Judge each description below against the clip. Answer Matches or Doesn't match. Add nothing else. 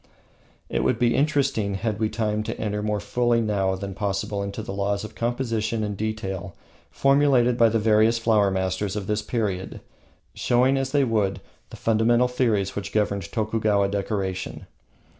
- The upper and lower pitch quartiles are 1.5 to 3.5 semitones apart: Matches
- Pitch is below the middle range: Matches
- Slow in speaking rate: Doesn't match